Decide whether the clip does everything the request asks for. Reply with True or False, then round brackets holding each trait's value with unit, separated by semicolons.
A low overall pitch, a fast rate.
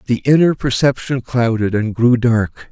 False (120 Hz; 155 wpm)